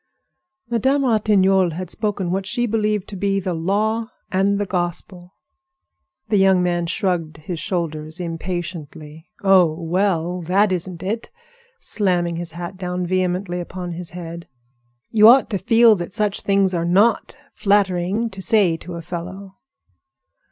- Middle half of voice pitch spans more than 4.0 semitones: No, average, 2.8 semitones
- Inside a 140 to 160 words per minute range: Yes, average, 145 wpm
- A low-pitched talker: No, medium, 185 Hz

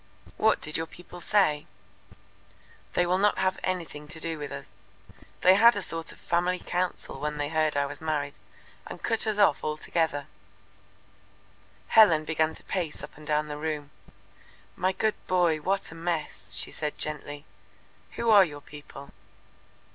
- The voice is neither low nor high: Yes, medium, 160 Hz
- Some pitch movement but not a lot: Yes, average, 3.5 semitones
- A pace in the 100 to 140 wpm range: No, average, 160 wpm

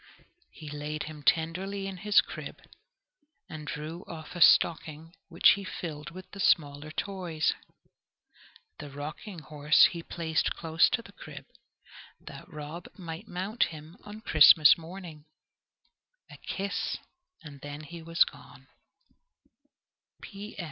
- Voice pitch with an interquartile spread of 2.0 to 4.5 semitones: Yes, average, 3.3 semitones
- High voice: No, medium, 165 Hz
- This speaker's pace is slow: Yes, slow, 120 wpm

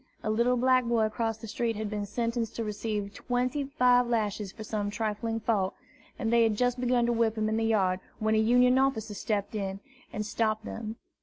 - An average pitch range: No, narrow, 2.1 semitones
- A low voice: No, high, 225 Hz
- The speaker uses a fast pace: Yes, fast, 210 wpm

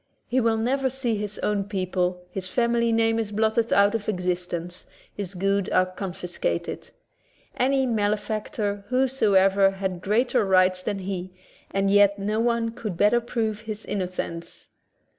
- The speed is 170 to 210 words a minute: No, average, 145 wpm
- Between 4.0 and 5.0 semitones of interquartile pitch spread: No, average, 3.3 semitones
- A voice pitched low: No, high, 205 Hz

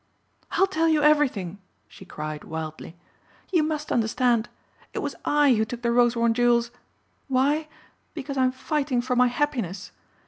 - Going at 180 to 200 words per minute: No, average, 150 wpm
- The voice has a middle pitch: No, very high, 250 Hz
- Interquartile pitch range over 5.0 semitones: No, average, 4.3 semitones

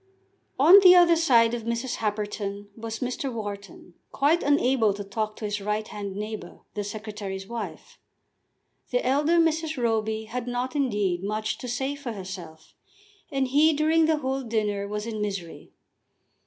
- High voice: Yes, high, 225 Hz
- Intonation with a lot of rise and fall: No, average, 4.7 semitones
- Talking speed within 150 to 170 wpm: Yes, average, 155 wpm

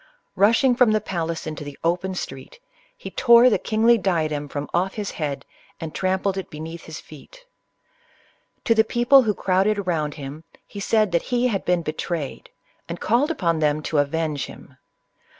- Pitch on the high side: No, medium, 180 Hz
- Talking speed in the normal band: Yes, average, 175 wpm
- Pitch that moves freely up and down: Yes, wide, 5.8 semitones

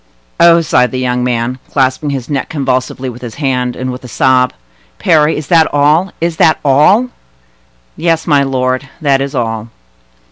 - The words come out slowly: No, average, 165 wpm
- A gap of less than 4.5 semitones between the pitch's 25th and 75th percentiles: Yes, average, 3.2 semitones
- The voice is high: No, low, 135 Hz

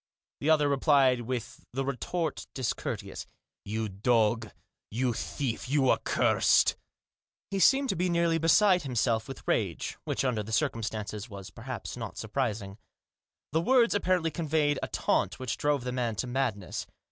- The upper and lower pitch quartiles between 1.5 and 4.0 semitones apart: No, wide, 5.6 semitones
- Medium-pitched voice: No, low, 130 Hz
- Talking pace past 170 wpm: No, average, 160 wpm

